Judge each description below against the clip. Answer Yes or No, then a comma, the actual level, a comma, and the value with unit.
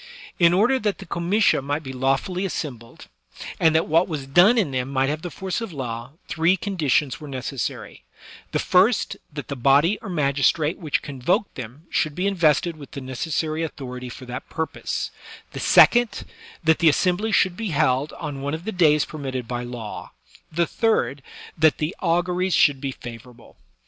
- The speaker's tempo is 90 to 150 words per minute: No, average, 180 wpm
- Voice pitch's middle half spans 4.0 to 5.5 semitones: Yes, average, 4.8 semitones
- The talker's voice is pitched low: No, medium, 155 Hz